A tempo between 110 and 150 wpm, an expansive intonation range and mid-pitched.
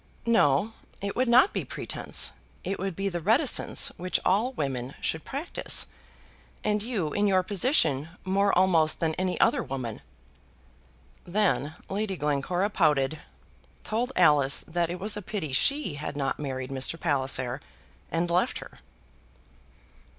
Yes: average, 140 wpm; wide, 6.2 semitones; medium, 180 Hz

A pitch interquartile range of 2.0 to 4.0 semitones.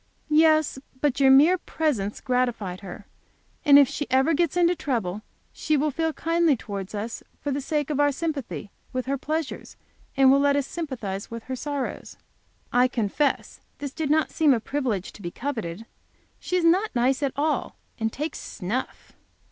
No: average, 4.6 semitones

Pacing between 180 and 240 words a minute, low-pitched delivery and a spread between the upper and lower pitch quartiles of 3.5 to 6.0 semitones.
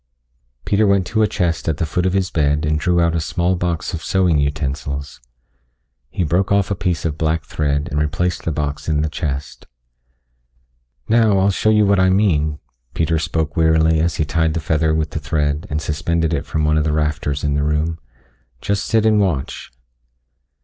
No: average, 200 wpm; very low, 80 Hz; average, 3.1 semitones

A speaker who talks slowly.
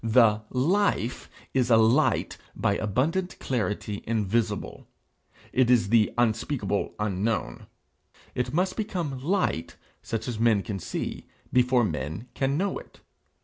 Yes: slow, 125 wpm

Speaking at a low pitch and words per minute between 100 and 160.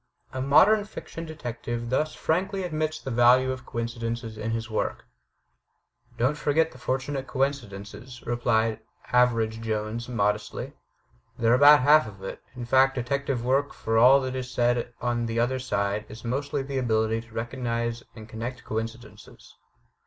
Yes: low, 120 Hz; average, 150 wpm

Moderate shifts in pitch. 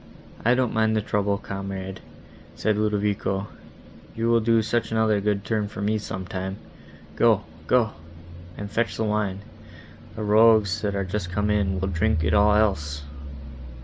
No: narrow, 2.0 semitones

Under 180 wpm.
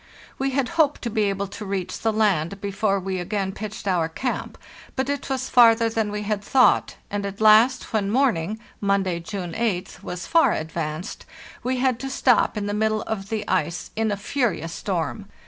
No: average, 190 wpm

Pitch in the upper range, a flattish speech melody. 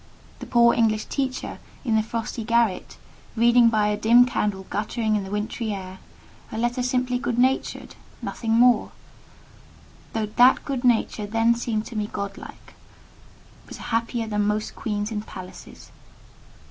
Yes: high, 225 Hz; narrow, 2.3 semitones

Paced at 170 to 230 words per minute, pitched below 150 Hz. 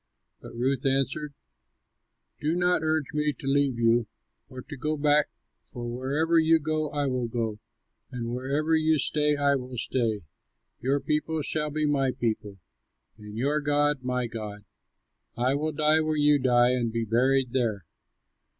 No: average, 160 wpm; low, 135 Hz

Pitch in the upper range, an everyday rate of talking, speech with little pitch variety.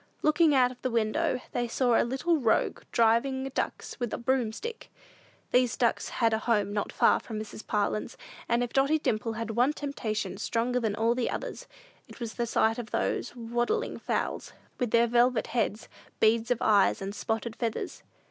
Yes: high, 235 Hz; average, 175 wpm; narrow, 2.3 semitones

